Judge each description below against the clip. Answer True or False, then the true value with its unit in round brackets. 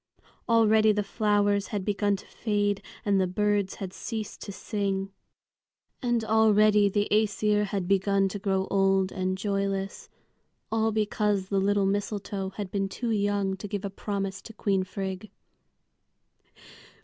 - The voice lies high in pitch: True (200 Hz)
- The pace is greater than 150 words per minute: False (145 wpm)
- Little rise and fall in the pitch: True (1.4 semitones)